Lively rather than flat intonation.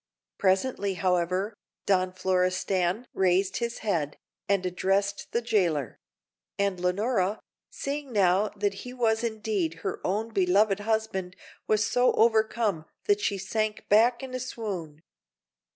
No: average, 3.3 semitones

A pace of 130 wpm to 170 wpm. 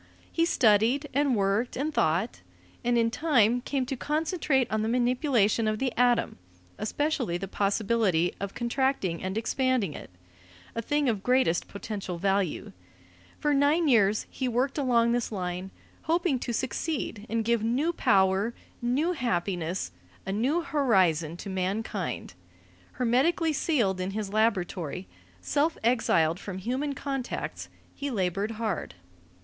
Yes: slow, 135 wpm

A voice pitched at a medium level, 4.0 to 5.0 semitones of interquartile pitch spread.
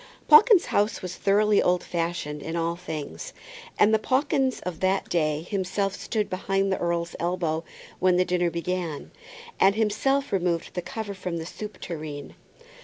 No: medium, 180 Hz; average, 3.6 semitones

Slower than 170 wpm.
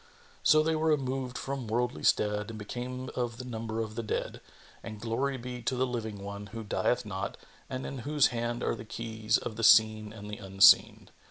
No: average, 200 wpm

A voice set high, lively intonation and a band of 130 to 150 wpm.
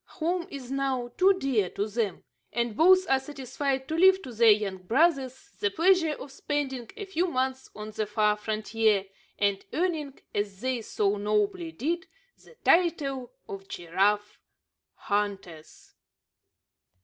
Yes: very high, 255 Hz; wide, 6.7 semitones; average, 140 wpm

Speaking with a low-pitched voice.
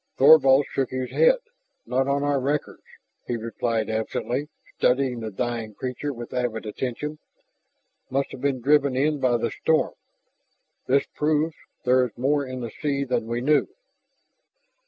Yes: low, 130 Hz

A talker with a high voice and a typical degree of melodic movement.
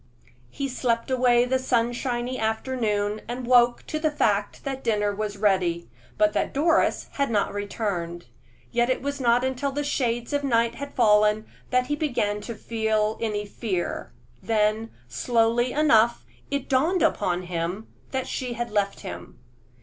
Yes: high, 230 Hz; average, 3.6 semitones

